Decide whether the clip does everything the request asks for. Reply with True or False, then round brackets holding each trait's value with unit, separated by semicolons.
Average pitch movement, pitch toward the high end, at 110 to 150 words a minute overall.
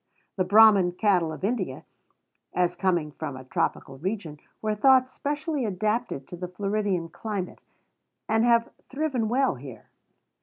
True (4.7 semitones; 200 Hz; 140 wpm)